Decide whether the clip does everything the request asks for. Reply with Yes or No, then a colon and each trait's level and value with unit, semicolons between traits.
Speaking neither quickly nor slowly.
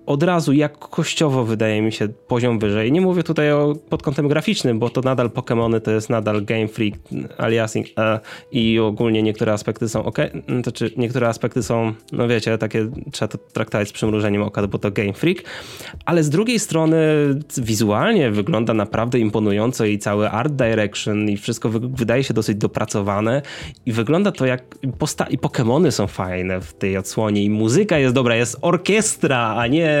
No: fast, 175 wpm